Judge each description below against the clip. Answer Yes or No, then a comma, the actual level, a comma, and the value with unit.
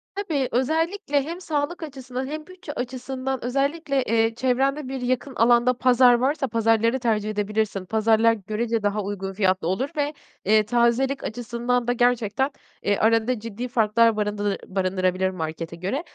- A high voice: Yes, high, 240 Hz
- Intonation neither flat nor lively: Yes, average, 3.9 semitones